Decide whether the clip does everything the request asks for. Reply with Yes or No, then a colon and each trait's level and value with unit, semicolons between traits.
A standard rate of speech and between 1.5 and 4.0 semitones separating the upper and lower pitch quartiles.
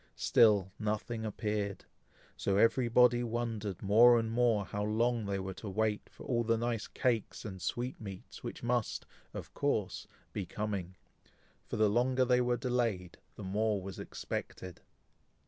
Yes: average, 150 wpm; average, 2.9 semitones